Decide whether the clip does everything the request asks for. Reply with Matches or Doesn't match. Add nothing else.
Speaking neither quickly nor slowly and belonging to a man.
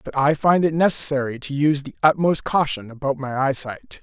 Matches